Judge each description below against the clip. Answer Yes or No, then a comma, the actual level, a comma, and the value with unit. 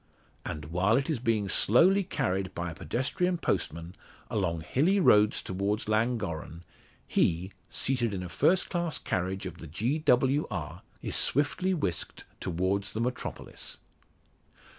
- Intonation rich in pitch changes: Yes, wide, 6.9 semitones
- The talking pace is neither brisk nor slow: No, slow, 130 wpm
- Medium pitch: No, low, 105 Hz